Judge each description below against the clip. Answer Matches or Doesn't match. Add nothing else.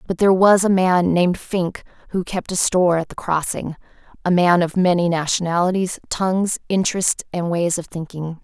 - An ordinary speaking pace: Matches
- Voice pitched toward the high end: Doesn't match